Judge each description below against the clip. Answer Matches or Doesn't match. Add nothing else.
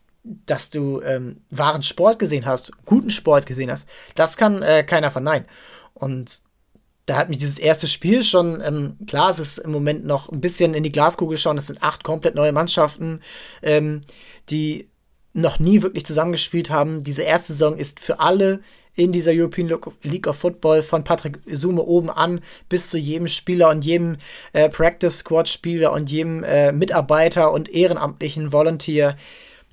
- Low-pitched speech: Doesn't match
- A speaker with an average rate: Matches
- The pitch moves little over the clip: Matches